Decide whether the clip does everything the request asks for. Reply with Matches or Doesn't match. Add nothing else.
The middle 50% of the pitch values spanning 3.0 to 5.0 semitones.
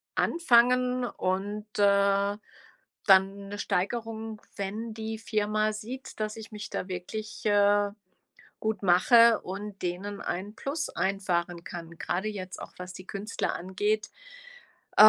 Doesn't match